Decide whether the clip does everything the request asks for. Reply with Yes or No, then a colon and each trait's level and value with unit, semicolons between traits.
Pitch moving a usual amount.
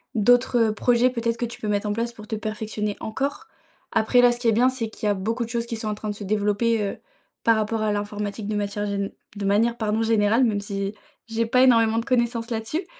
No: narrow, 2.1 semitones